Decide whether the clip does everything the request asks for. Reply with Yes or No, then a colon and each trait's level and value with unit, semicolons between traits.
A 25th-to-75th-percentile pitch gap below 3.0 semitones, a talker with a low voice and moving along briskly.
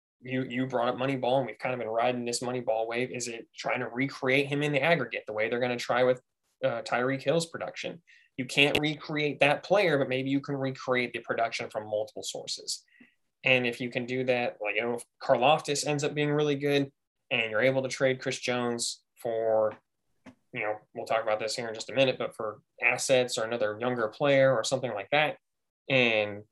Yes: narrow, 2.5 semitones; low, 125 Hz; fast, 220 wpm